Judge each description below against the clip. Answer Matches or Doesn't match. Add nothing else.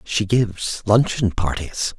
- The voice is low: Matches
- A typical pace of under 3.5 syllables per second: Doesn't match